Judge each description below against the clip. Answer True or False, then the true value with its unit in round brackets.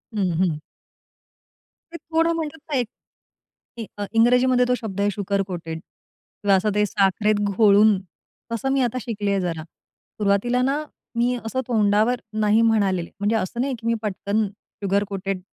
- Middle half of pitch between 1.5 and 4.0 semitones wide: True (3.5 semitones)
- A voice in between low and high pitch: False (210 Hz)